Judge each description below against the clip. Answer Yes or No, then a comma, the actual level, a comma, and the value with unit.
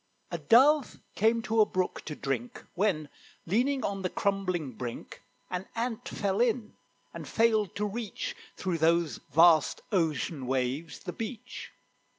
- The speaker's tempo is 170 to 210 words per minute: No, average, 145 wpm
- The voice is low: No, high, 190 Hz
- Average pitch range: No, wide, 6.1 semitones